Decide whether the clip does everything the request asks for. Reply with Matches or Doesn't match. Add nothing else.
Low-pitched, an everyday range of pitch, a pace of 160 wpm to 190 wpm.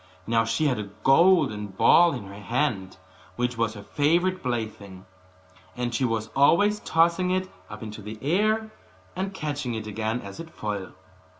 Doesn't match